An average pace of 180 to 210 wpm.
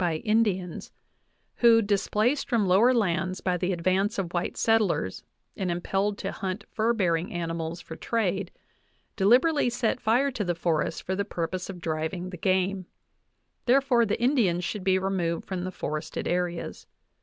No: average, 160 wpm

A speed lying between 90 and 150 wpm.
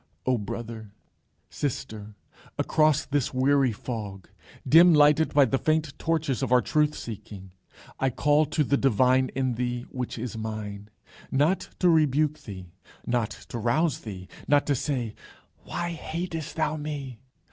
Yes: average, 145 wpm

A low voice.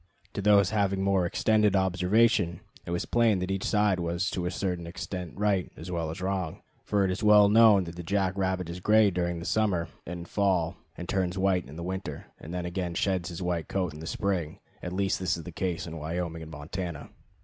Yes: very low, 90 Hz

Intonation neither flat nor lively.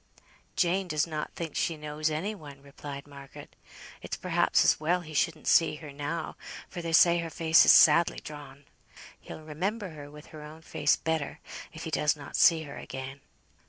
No: narrow, 2.1 semitones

